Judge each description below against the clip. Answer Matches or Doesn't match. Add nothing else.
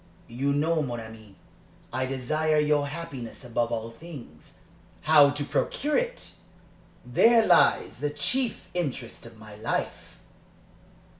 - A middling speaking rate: Doesn't match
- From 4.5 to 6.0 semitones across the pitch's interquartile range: Matches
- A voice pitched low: Doesn't match